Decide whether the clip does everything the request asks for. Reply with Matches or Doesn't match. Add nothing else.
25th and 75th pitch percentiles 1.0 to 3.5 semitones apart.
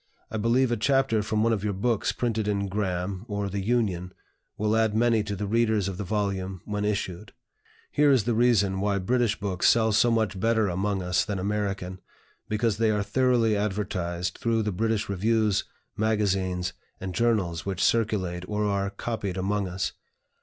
Matches